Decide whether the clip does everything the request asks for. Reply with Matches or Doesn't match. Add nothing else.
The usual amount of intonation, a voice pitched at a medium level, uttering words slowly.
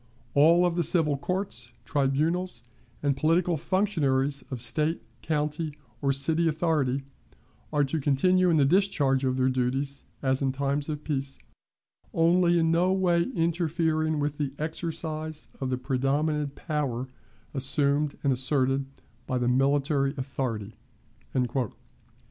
Matches